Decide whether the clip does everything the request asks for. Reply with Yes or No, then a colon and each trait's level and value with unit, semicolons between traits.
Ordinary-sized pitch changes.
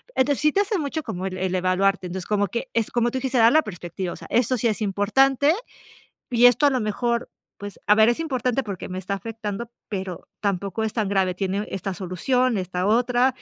Yes: average, 4.6 semitones